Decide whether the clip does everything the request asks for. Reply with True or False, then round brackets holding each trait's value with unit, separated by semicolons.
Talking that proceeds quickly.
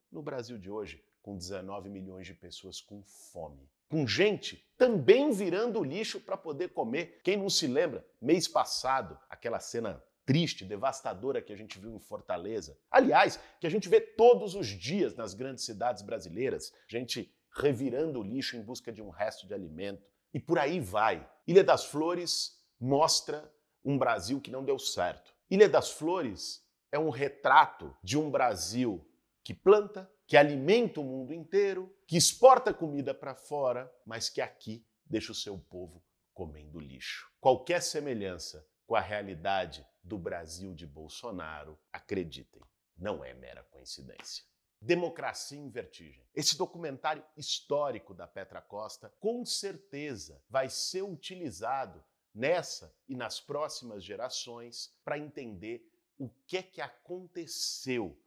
False (145 wpm)